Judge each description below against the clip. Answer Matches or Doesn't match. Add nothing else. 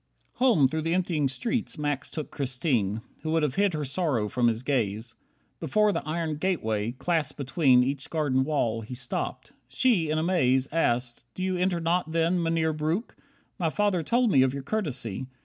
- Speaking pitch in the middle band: Matches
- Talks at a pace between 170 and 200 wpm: Matches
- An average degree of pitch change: Matches